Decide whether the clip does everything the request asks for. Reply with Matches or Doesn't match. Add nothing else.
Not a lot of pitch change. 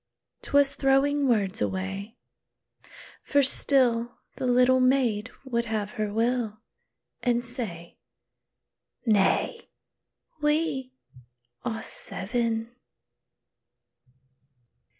Doesn't match